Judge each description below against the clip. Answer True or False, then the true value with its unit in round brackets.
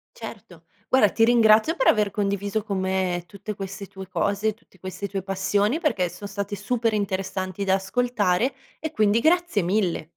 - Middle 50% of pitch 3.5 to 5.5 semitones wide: False (2.4 semitones)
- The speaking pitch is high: True (200 Hz)